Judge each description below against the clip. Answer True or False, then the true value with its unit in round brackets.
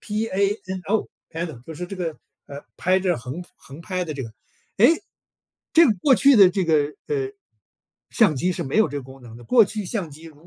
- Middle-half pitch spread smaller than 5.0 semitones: False (5.6 semitones)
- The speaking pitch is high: False (180 Hz)